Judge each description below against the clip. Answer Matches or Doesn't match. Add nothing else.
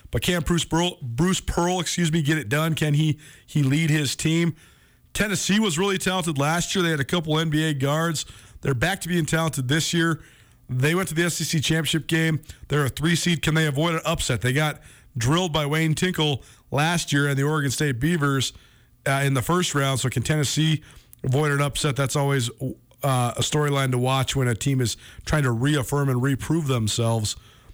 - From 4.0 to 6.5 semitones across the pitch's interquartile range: Doesn't match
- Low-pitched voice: Doesn't match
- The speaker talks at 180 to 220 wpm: Matches